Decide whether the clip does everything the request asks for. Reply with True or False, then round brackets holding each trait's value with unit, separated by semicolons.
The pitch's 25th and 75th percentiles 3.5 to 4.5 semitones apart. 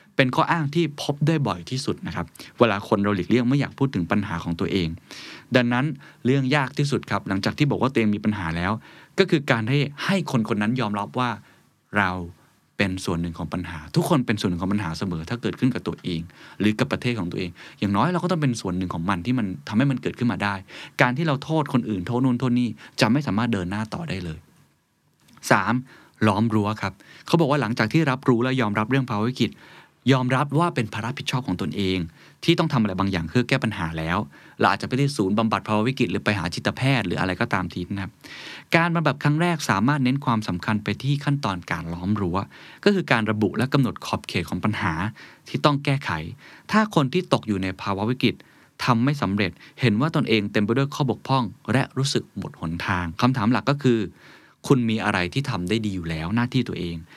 False (5.4 semitones)